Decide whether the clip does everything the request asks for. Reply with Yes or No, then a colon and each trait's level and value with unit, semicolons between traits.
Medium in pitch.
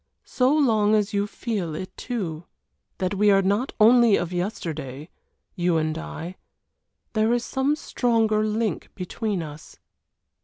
No: high, 205 Hz